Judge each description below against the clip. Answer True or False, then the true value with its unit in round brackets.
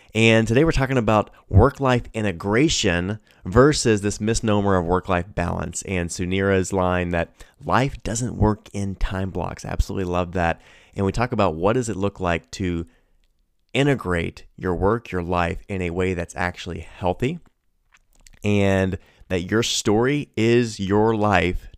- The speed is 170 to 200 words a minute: False (155 wpm)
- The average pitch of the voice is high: False (100 Hz)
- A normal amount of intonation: True (4.0 semitones)